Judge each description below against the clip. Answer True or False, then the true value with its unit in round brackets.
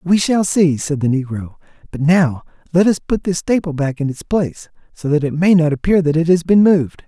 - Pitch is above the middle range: False (160 Hz)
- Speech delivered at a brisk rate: True (235 wpm)